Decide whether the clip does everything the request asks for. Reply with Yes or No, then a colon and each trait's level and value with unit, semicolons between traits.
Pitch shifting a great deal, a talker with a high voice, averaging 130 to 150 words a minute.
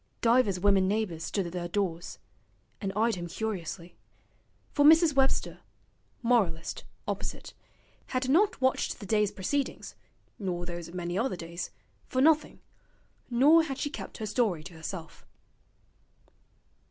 Yes: wide, 6.7 semitones; high, 205 Hz; slow, 135 wpm